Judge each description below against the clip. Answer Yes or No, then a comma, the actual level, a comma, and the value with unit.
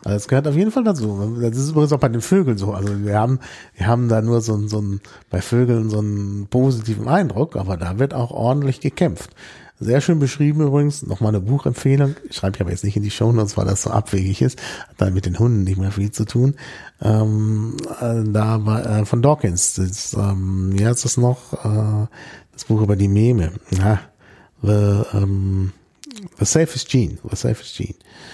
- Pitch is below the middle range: Yes, low, 110 Hz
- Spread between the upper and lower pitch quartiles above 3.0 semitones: Yes, average, 4.2 semitones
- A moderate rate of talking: No, fast, 200 wpm